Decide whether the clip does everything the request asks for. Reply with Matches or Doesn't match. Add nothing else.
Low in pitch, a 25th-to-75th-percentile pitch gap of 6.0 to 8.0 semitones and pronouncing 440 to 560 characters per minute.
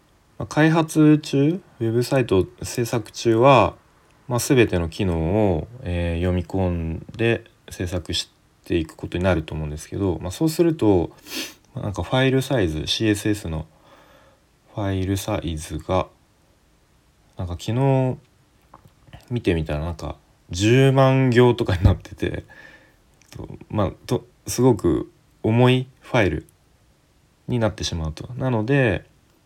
Doesn't match